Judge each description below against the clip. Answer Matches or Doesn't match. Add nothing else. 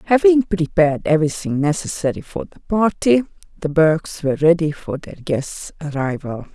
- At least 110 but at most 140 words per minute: Matches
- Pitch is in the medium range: Matches